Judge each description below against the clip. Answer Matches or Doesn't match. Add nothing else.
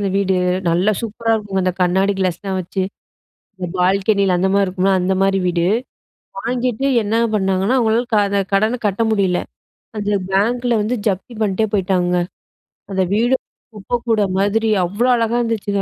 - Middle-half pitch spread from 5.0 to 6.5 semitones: Doesn't match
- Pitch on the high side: Matches